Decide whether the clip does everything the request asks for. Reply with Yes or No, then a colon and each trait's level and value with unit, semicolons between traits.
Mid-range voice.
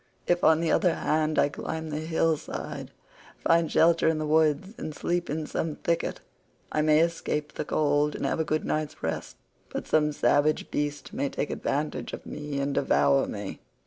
Yes: medium, 155 Hz